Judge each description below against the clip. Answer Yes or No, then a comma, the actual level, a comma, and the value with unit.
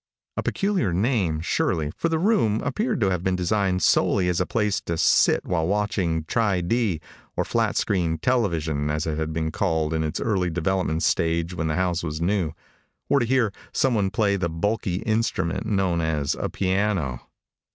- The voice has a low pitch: Yes, very low, 90 Hz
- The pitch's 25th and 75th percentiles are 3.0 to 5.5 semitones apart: Yes, average, 4.5 semitones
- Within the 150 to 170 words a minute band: No, average, 180 wpm